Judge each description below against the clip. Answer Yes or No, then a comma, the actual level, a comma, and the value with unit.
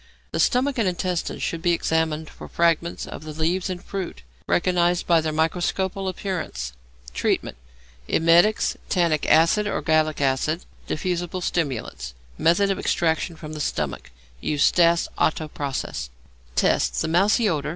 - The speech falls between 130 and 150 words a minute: Yes, average, 140 wpm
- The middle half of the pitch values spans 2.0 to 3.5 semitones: Yes, average, 2.8 semitones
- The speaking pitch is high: No, medium, 165 Hz